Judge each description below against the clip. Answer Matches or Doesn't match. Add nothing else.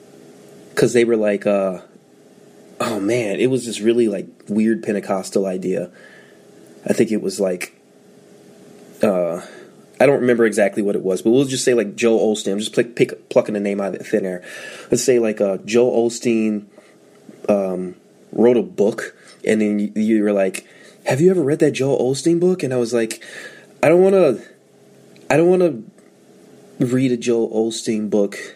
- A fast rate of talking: Doesn't match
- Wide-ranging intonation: Doesn't match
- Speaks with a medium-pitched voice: Doesn't match